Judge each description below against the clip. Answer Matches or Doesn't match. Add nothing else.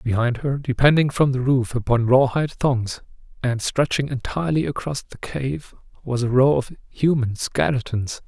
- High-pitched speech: Doesn't match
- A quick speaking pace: Doesn't match